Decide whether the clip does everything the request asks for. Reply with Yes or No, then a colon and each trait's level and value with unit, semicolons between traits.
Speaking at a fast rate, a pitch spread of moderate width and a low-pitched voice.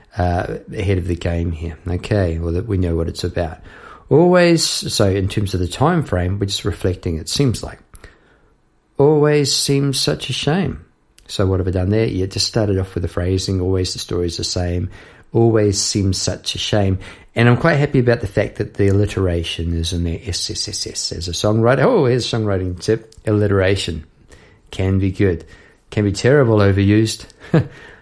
No: average, 185 wpm; average, 4.2 semitones; low, 100 Hz